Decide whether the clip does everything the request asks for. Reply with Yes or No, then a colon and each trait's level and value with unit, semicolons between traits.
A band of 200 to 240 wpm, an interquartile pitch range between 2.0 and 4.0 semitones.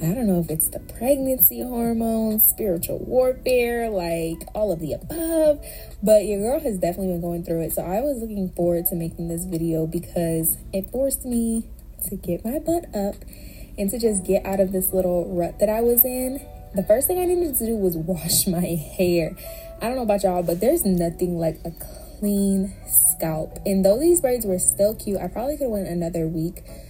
No: fast, 205 wpm; average, 5.2 semitones